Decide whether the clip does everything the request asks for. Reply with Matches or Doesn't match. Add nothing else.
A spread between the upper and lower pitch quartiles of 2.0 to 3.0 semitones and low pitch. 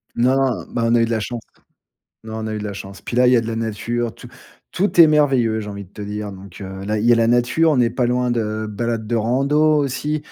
Matches